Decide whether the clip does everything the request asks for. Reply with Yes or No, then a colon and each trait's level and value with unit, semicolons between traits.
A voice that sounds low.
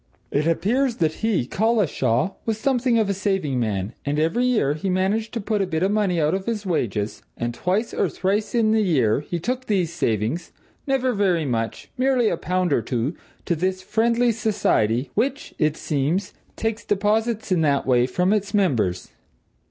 No: medium, 185 Hz